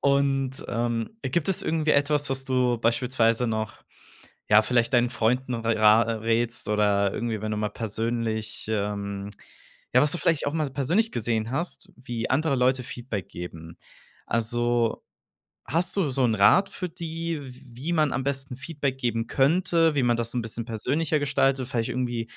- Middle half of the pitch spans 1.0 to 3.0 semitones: No, average, 3.8 semitones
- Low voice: Yes, low, 125 Hz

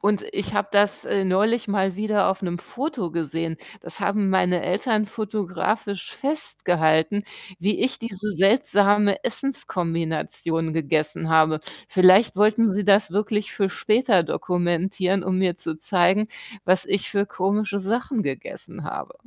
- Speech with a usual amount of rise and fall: Yes, average, 3.2 semitones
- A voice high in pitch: Yes, high, 195 Hz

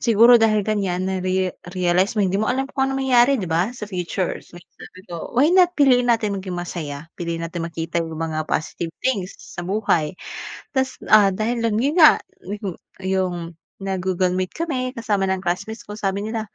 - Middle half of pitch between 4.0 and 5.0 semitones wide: Yes, average, 4.4 semitones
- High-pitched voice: Yes, high, 195 Hz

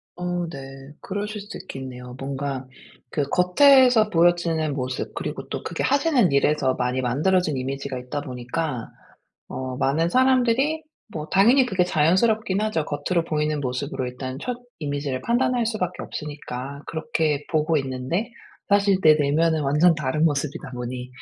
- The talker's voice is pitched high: No, medium, 155 Hz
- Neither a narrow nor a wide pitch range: No, wide, 5.9 semitones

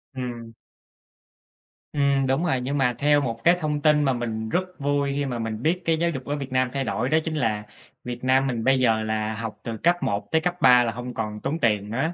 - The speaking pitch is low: Yes, low, 130 Hz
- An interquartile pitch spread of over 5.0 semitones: No, average, 4.1 semitones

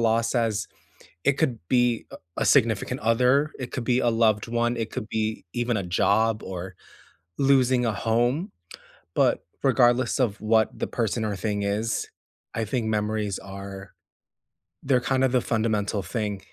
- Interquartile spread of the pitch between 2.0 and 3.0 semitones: Yes, narrow, 2.6 semitones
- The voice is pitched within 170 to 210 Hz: No, low, 115 Hz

